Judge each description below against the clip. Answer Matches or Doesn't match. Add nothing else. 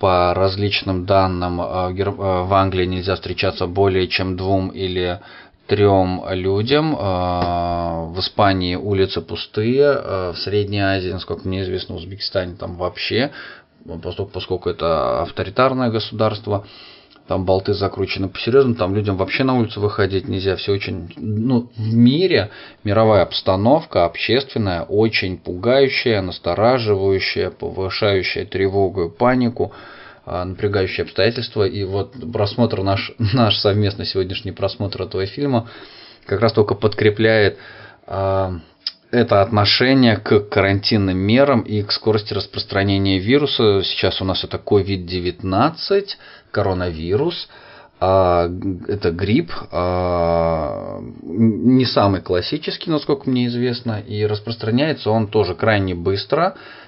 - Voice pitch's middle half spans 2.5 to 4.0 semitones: Matches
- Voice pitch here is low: Matches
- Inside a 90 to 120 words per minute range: Matches